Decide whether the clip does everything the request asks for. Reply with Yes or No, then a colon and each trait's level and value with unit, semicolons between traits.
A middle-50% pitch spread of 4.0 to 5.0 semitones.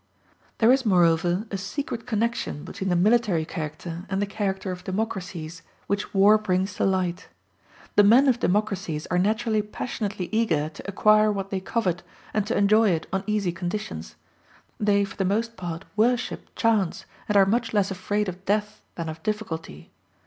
No: average, 3.1 semitones